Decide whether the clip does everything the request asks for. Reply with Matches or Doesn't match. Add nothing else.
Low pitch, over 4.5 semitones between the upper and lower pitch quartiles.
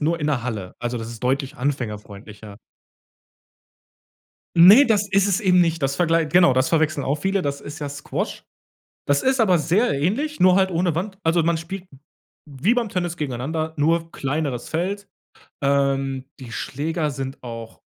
Doesn't match